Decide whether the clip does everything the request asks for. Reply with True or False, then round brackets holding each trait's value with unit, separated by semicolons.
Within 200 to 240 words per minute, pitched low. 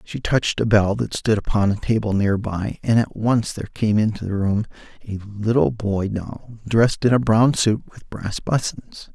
True (205 wpm; 110 Hz)